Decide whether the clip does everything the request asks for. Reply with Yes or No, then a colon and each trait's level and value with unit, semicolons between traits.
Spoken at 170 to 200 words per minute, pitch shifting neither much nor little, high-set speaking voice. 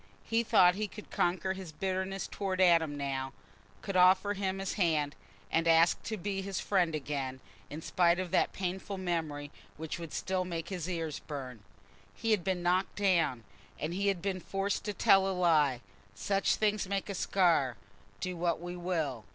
No: average, 175 wpm; average, 3.1 semitones; medium, 180 Hz